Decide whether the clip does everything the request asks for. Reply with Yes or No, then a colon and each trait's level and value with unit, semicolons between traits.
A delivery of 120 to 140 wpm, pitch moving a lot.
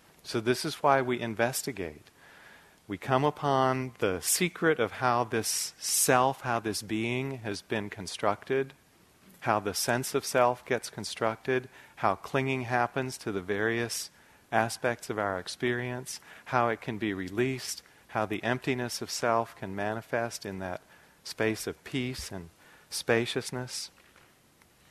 No: slow, 135 wpm; average, 3.2 semitones